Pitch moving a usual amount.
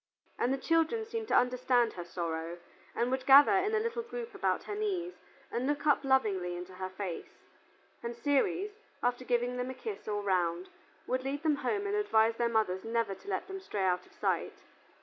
No: wide, 8.9 semitones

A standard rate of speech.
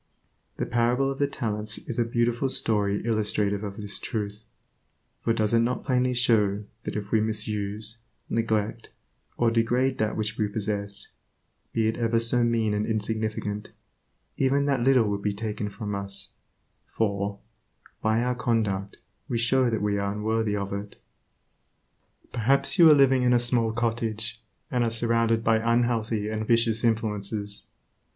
Yes: average, 155 wpm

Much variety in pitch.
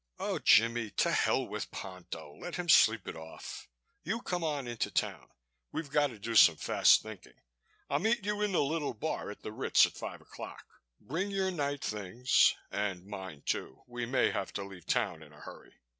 Yes: wide, 8.3 semitones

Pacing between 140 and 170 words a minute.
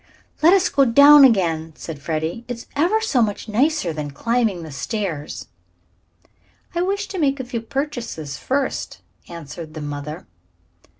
Yes: average, 145 wpm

